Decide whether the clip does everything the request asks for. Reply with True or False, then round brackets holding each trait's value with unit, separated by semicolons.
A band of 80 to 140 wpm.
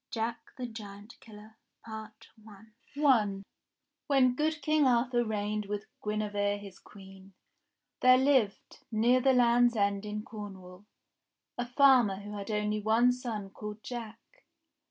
True (135 wpm)